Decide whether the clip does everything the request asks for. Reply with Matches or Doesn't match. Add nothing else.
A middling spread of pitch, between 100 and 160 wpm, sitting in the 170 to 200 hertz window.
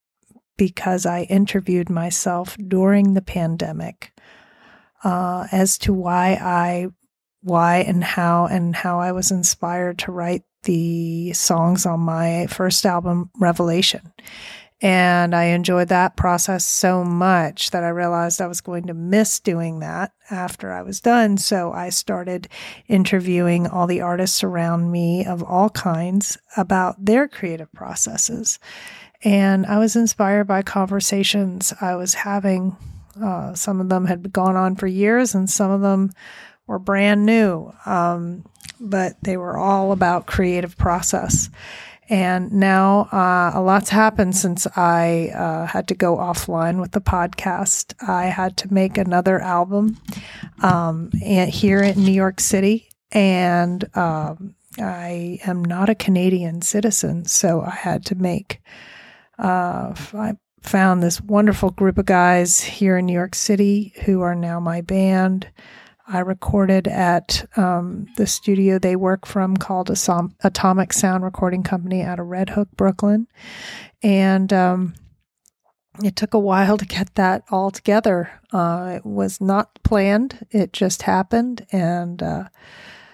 Doesn't match